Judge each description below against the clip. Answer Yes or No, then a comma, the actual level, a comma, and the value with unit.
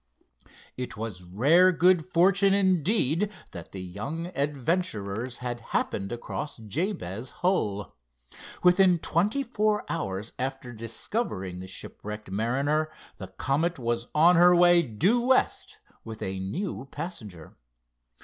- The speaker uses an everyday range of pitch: No, wide, 8.9 semitones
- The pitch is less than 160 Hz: Yes, medium, 140 Hz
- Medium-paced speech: No, slow, 120 wpm